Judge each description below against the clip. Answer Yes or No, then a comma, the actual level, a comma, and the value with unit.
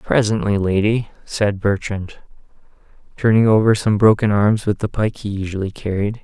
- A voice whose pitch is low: Yes, low, 105 Hz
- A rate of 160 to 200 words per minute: No, average, 145 wpm